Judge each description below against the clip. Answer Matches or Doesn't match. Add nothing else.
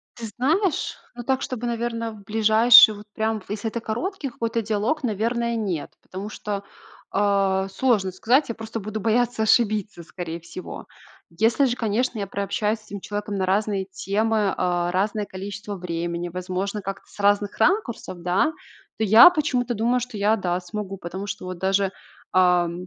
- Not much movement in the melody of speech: Doesn't match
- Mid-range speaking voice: Doesn't match